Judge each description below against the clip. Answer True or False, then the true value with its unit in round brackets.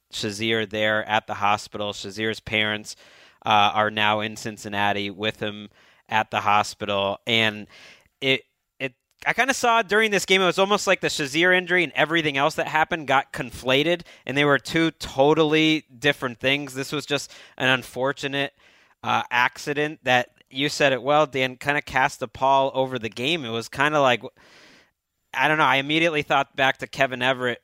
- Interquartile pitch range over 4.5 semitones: True (5.6 semitones)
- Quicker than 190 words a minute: False (180 wpm)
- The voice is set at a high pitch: False (135 Hz)